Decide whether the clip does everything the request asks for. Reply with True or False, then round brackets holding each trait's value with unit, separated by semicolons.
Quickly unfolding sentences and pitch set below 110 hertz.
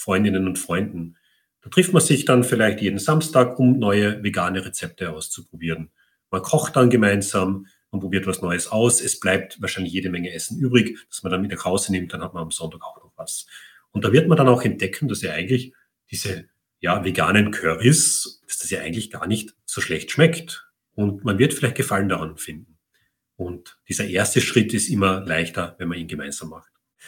True (195 wpm; 100 Hz)